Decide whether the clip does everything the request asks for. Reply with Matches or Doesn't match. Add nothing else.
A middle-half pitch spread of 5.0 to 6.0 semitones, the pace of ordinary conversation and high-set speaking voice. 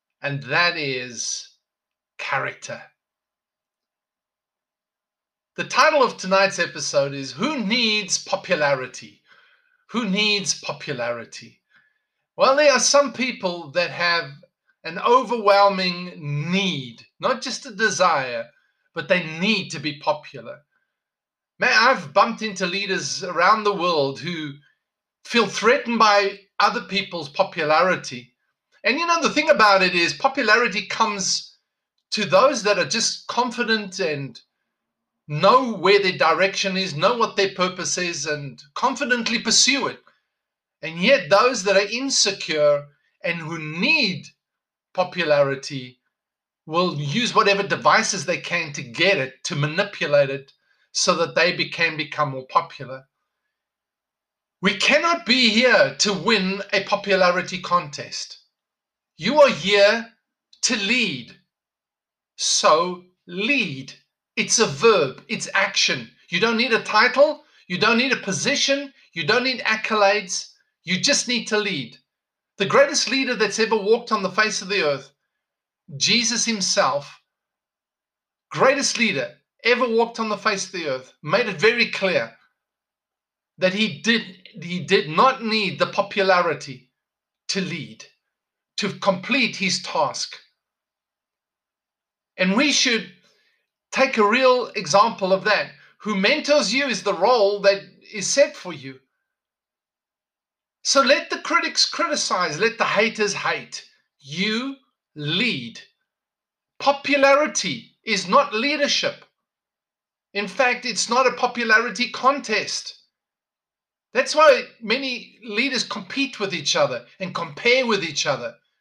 Doesn't match